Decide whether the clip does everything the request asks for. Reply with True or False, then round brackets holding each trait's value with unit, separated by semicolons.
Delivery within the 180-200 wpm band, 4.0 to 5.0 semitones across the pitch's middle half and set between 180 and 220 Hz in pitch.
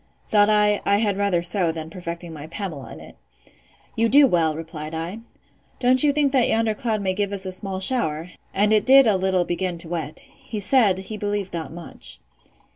True (190 wpm; 4.3 semitones; 190 Hz)